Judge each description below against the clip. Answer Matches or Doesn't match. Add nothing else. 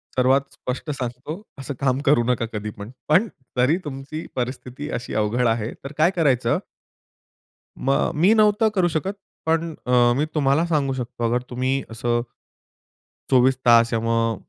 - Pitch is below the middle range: Matches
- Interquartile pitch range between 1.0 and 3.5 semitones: Doesn't match